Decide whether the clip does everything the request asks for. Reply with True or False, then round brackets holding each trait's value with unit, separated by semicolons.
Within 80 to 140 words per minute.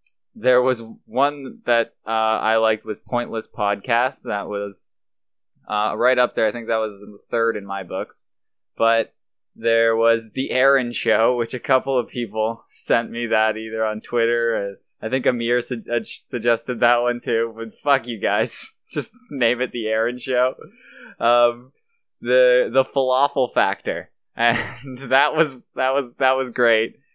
False (165 wpm)